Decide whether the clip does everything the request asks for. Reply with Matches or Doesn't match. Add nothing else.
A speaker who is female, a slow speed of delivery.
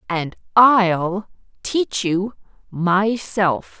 Matches